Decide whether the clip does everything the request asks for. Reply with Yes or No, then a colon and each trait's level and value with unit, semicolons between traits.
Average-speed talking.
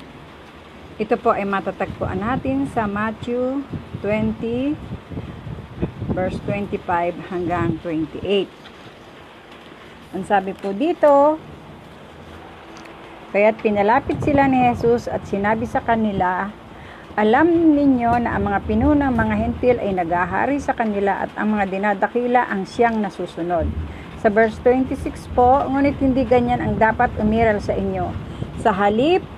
No: slow, 120 wpm